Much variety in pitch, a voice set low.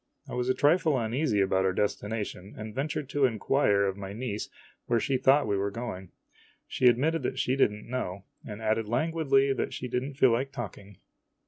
No: average, 4.7 semitones; low, 120 Hz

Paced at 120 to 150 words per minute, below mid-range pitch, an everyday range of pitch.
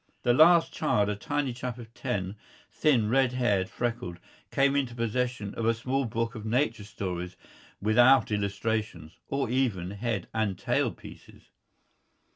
Yes: average, 145 wpm; low, 115 Hz; average, 3.7 semitones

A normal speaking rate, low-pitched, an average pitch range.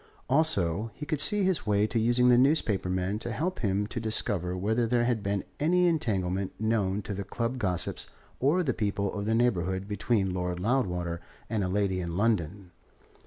Yes: average, 185 wpm; low, 105 Hz; average, 4.5 semitones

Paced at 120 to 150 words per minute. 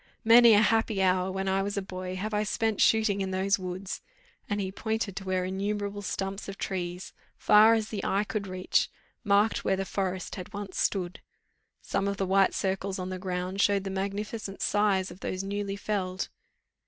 No: average, 190 wpm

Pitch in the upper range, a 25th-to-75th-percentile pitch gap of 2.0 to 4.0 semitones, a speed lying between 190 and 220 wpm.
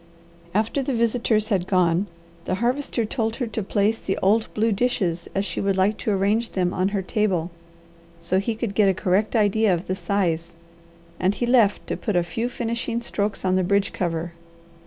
Yes: high, 200 Hz; average, 3.4 semitones; average, 195 wpm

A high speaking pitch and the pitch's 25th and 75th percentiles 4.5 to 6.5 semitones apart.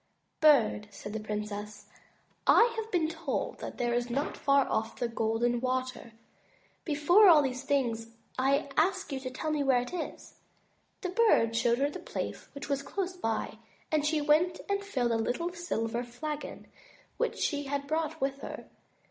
Yes: very high, 280 Hz; average, 5.0 semitones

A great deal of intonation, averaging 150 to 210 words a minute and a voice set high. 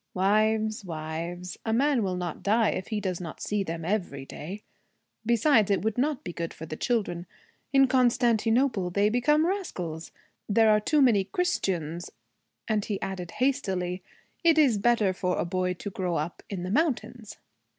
No: average, 5.0 semitones; average, 170 wpm; high, 205 Hz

